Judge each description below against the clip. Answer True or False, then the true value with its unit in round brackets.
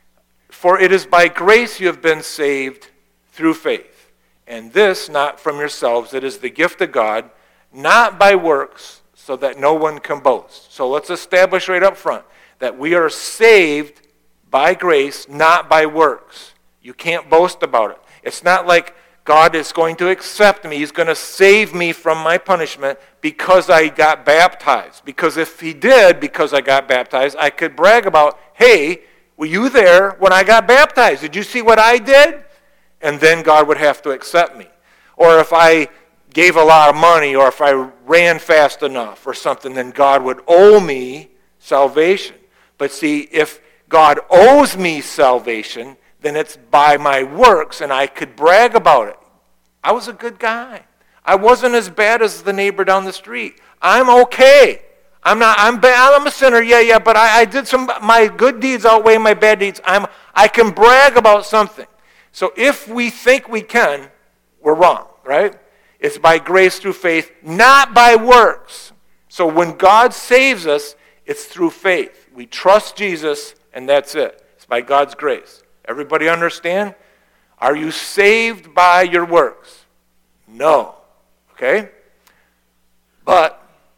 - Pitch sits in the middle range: True (180 Hz)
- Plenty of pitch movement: True (7.3 semitones)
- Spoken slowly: False (170 wpm)